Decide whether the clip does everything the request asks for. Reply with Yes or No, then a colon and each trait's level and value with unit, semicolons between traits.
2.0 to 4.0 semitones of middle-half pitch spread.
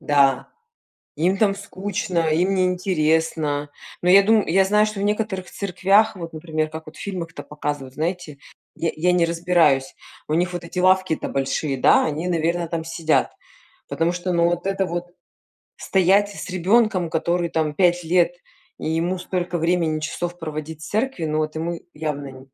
Yes: average, 2.9 semitones